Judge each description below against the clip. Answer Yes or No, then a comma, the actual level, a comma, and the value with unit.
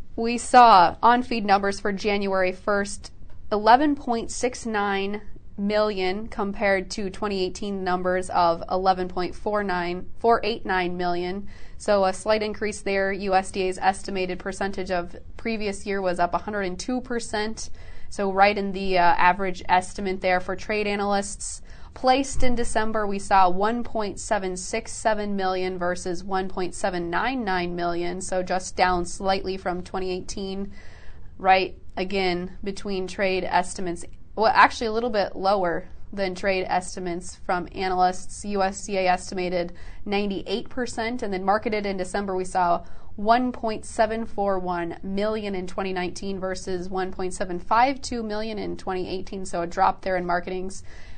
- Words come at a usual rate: No, slow, 115 wpm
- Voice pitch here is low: No, high, 195 Hz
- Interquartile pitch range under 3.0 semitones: Yes, narrow, 2.4 semitones